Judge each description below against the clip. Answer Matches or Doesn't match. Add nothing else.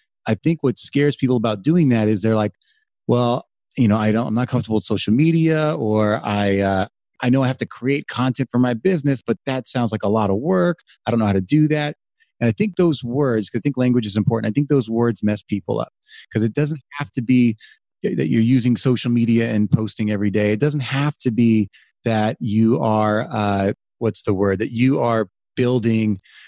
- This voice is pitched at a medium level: Doesn't match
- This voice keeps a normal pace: Doesn't match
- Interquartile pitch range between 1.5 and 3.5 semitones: Doesn't match